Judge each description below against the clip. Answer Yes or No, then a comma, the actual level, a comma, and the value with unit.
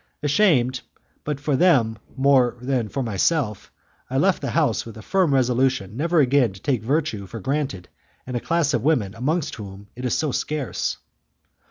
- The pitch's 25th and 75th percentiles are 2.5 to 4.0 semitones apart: No, average, 4.7 semitones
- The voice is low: Yes, low, 130 Hz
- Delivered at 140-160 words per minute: No, average, 170 wpm